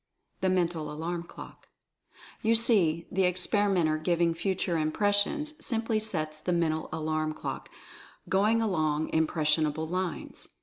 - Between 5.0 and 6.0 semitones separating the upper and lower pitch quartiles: No, average, 4.5 semitones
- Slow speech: Yes, slow, 125 wpm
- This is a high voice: No, medium, 170 Hz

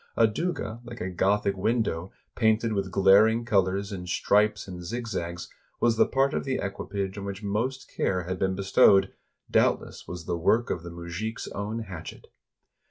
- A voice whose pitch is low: Yes, low, 100 Hz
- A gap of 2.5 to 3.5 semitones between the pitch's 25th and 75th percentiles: Yes, average, 3.2 semitones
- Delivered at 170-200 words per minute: Yes, average, 175 wpm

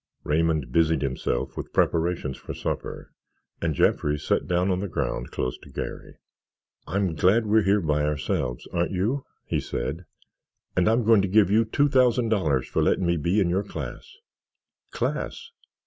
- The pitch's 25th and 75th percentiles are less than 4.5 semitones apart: No, wide, 5.4 semitones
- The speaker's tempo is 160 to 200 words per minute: Yes, average, 165 wpm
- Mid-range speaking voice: No, very low, 90 Hz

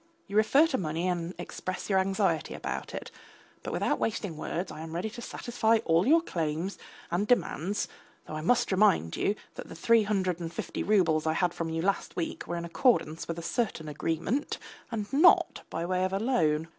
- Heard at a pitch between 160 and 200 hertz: Yes, medium, 185 Hz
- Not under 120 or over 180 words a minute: No, average, 200 wpm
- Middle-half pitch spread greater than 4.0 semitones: Yes, average, 4.5 semitones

